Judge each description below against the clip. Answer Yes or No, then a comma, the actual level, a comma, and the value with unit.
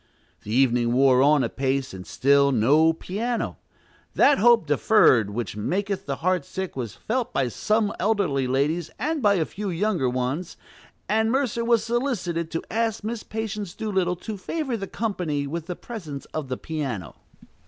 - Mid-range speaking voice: Yes, medium, 175 Hz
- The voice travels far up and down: Yes, wide, 7.9 semitones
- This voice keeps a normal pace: Yes, average, 165 wpm